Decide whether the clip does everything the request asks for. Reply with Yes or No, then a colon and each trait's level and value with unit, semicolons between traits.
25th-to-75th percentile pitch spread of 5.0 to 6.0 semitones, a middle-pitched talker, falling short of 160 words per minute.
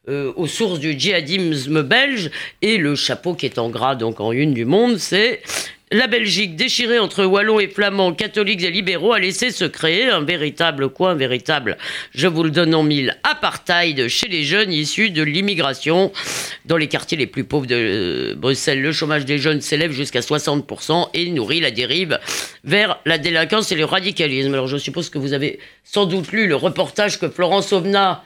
No: average, 5.3 semitones; medium, 165 Hz; average, 190 wpm